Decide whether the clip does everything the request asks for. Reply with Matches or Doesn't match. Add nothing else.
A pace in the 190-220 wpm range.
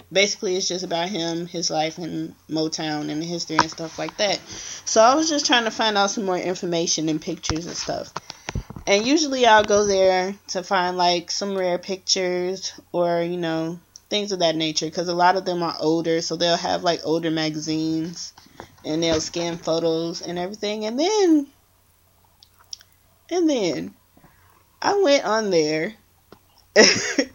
Doesn't match